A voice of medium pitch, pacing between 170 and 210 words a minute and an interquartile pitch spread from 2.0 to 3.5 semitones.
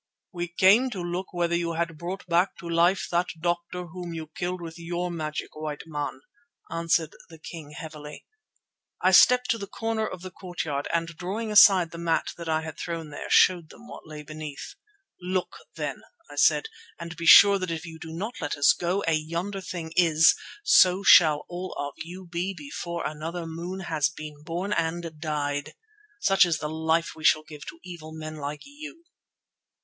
Yes: medium, 170 Hz; average, 190 wpm; narrow, 2.4 semitones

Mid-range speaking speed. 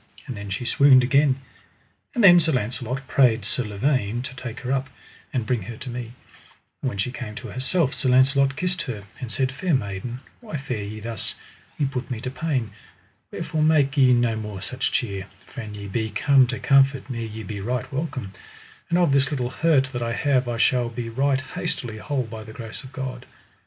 No: fast, 210 wpm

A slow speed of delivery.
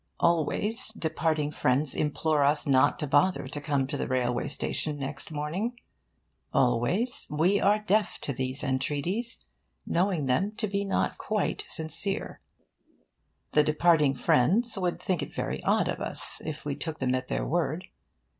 No: average, 155 wpm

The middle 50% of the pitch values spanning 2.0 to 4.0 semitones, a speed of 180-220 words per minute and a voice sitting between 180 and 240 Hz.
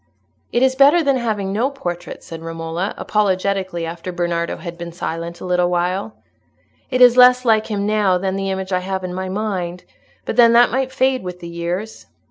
No: average, 4.8 semitones; average, 195 wpm; high, 190 Hz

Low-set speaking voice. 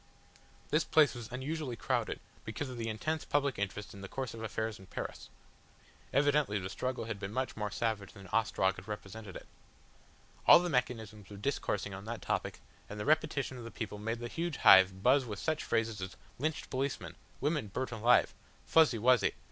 Yes: low, 115 Hz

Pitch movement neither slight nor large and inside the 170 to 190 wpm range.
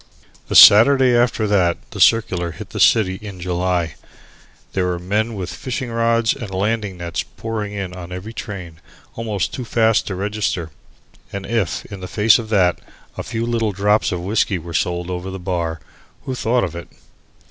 Yes: average, 4.0 semitones; average, 175 wpm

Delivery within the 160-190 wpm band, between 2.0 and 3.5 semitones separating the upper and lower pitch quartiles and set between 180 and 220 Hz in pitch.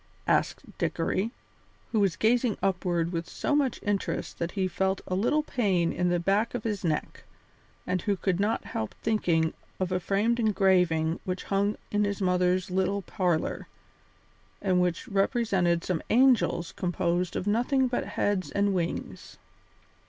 No: average, 150 wpm; average, 2.9 semitones; high, 190 Hz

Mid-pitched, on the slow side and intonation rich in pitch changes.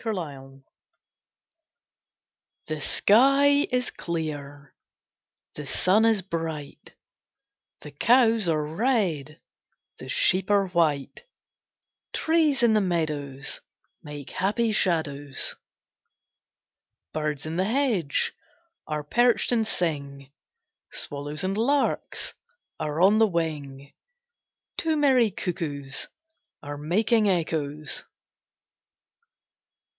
Yes: medium, 170 Hz; slow, 95 wpm; wide, 7.1 semitones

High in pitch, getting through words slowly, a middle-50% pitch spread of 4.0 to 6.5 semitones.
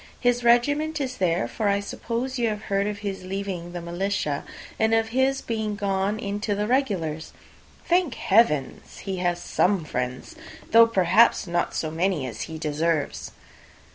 No: high, 200 Hz; average, 160 wpm; average, 5.0 semitones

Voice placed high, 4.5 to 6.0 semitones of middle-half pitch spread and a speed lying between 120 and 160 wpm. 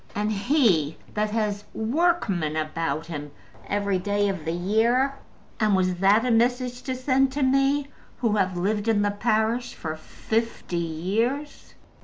Yes: high, 210 Hz; average, 5.1 semitones; average, 150 wpm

